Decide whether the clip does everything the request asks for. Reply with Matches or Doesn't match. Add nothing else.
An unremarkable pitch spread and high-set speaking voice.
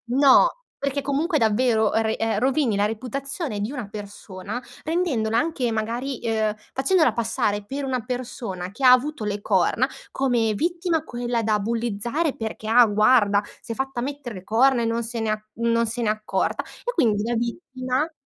Matches